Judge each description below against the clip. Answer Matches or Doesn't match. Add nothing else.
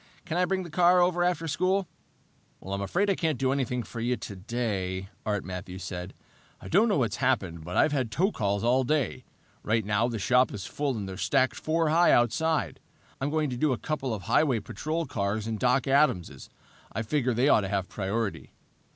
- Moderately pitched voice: Doesn't match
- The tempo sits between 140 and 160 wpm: Doesn't match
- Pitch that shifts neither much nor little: Doesn't match